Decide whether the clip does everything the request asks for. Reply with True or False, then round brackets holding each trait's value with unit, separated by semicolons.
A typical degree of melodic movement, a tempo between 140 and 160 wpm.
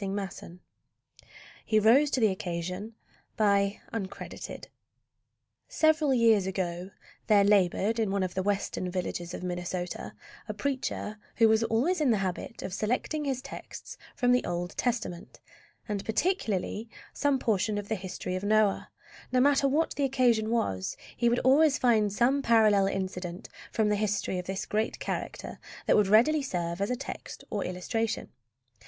True (4.7 semitones; 150 wpm)